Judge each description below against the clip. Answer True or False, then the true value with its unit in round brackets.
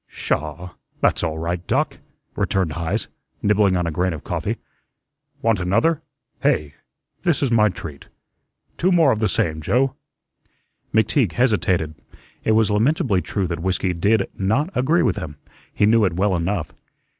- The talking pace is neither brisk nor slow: True (150 wpm)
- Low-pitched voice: True (95 Hz)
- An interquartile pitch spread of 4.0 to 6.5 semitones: True (5.1 semitones)